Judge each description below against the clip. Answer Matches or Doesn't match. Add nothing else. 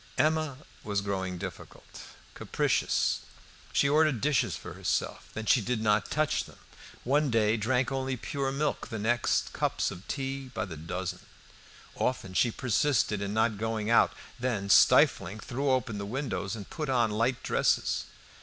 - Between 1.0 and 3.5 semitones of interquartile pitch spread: Doesn't match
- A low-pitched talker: Matches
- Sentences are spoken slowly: Doesn't match